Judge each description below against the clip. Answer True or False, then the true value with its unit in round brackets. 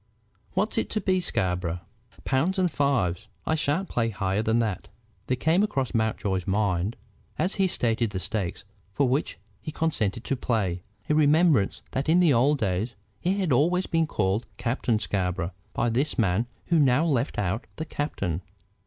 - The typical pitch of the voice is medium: False (120 Hz)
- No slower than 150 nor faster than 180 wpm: True (170 wpm)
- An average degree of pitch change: False (7.7 semitones)